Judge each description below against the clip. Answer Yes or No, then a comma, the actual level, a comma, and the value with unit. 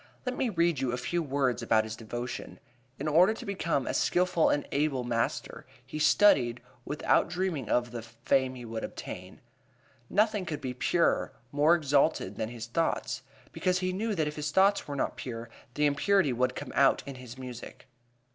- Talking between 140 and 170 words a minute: No, average, 185 wpm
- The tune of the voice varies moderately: No, wide, 6.0 semitones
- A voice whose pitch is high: No, medium, 140 Hz